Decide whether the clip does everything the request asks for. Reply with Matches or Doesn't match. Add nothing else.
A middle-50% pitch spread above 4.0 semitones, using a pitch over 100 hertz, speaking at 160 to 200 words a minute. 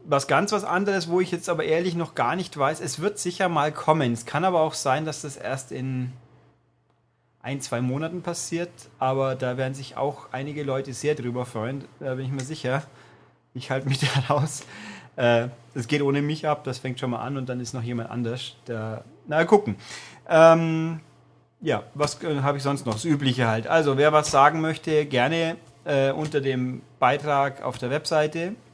Doesn't match